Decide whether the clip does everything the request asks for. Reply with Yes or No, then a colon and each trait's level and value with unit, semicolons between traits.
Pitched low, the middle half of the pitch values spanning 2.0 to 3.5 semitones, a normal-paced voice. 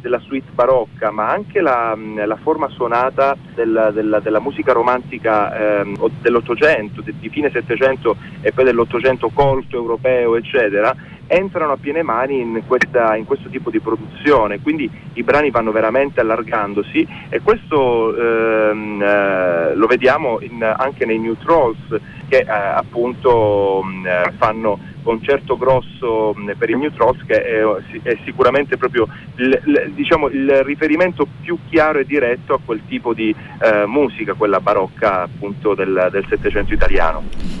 No: low, 120 Hz; average, 4.5 semitones; average, 145 wpm